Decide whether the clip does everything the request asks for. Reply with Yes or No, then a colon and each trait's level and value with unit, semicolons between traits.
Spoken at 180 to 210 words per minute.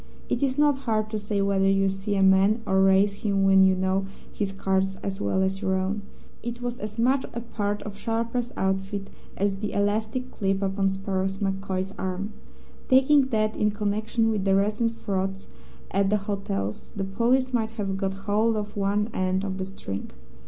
Yes: average, 190 wpm